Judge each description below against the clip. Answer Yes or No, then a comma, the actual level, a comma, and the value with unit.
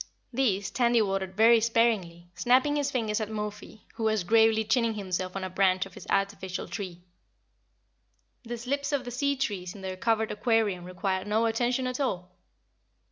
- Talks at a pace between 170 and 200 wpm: Yes, average, 175 wpm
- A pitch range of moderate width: Yes, average, 3.9 semitones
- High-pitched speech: Yes, high, 215 Hz